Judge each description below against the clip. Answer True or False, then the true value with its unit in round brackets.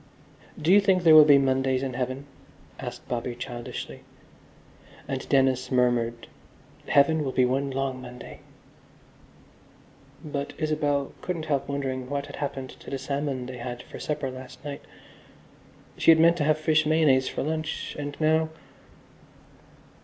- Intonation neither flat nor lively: True (3.0 semitones)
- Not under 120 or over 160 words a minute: True (145 wpm)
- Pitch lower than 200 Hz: True (140 Hz)